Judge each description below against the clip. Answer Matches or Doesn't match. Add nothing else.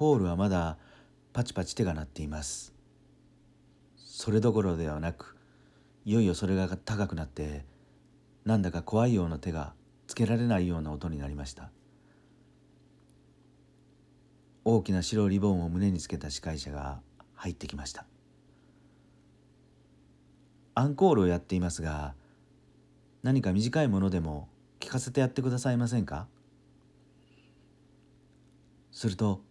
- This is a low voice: Matches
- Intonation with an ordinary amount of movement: Doesn't match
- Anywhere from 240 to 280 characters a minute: Matches